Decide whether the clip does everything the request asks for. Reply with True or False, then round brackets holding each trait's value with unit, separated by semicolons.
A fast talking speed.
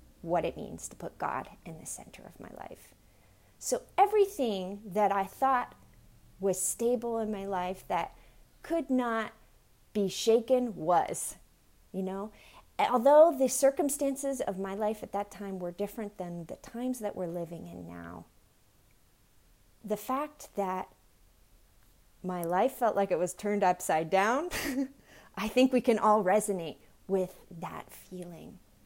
False (145 wpm)